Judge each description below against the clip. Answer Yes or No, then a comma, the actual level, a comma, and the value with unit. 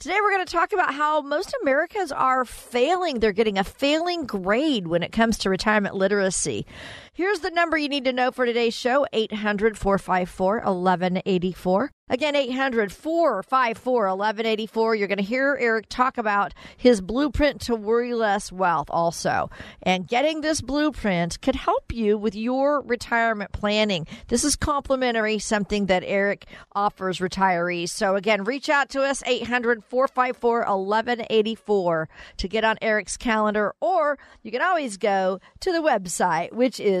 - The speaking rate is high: No, average, 145 wpm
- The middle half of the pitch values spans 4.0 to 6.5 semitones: Yes, wide, 5.4 semitones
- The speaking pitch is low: No, high, 225 Hz